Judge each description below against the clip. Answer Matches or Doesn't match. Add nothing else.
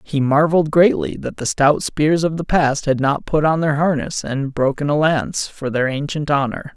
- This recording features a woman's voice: Doesn't match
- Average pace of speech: Doesn't match